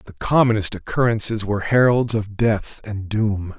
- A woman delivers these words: No, male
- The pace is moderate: Yes, average, 150 wpm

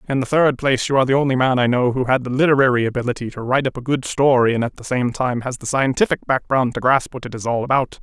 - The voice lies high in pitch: No, low, 130 Hz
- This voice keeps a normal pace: No, fast, 285 wpm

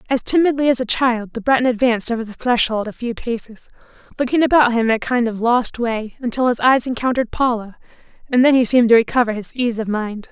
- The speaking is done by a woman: Yes, female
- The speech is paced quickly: Yes, fast, 220 wpm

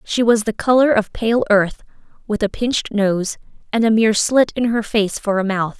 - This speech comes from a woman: Yes, female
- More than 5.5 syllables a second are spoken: No, 5.0 syllables/s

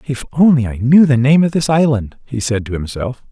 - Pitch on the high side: No, low, 130 Hz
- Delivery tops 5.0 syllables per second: Yes, 5.3 syllables/s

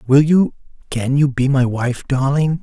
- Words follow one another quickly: No, average, 160 wpm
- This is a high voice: No, low, 135 Hz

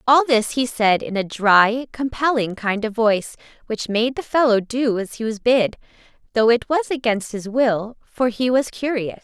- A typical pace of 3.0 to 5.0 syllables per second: Yes, 4.5 syllables/s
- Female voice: Yes, female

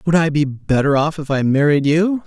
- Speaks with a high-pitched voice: No, medium, 150 Hz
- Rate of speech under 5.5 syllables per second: Yes, 5.1 syllables/s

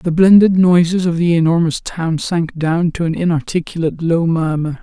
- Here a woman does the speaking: No, male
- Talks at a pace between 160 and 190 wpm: Yes, average, 175 wpm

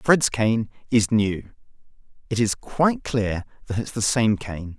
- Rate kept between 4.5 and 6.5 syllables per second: No, 4.1 syllables/s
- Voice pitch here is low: Yes, low, 110 Hz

